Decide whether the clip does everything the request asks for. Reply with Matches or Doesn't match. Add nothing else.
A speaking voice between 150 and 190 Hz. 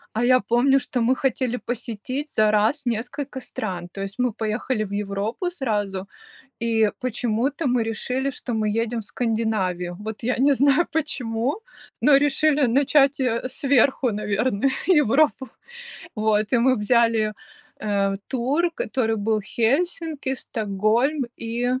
Doesn't match